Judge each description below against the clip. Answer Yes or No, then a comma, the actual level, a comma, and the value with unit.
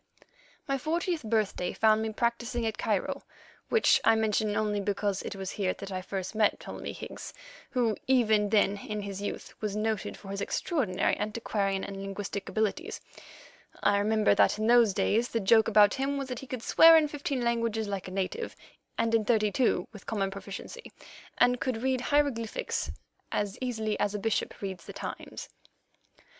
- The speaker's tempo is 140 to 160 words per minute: No, average, 175 wpm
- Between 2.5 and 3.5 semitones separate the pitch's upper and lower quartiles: Yes, average, 3.1 semitones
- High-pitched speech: Yes, high, 215 Hz